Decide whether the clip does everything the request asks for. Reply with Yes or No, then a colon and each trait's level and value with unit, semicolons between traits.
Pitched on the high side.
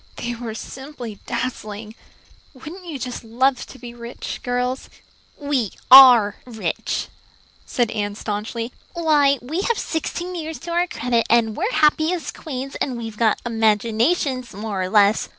Yes: high, 245 Hz